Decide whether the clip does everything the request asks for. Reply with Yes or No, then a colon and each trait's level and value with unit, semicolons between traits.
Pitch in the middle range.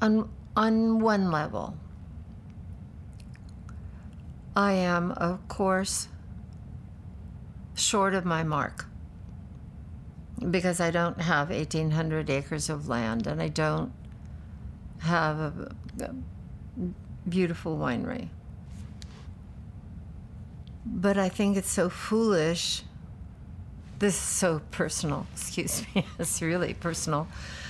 Yes: medium, 145 Hz